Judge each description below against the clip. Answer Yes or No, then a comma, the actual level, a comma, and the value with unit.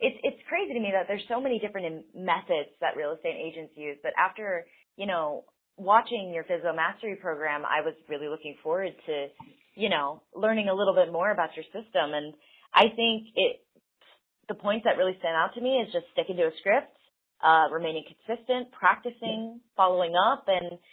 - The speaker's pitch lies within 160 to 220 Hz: Yes, high, 190 Hz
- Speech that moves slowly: No, average, 190 wpm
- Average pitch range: No, wide, 5.9 semitones